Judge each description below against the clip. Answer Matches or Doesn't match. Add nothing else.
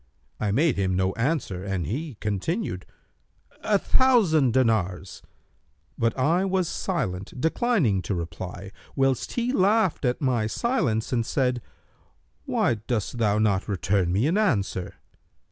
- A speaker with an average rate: Doesn't match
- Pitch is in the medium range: Doesn't match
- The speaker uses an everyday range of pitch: Doesn't match